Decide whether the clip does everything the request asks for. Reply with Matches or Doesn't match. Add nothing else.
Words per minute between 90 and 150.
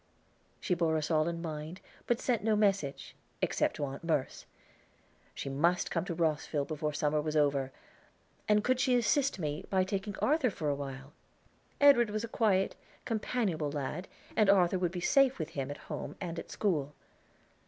Doesn't match